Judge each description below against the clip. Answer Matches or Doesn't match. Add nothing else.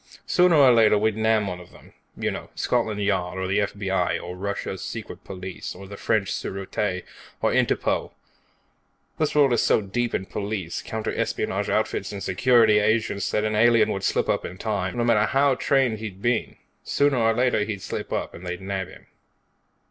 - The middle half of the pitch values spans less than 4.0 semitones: Matches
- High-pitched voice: Doesn't match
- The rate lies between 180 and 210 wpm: Matches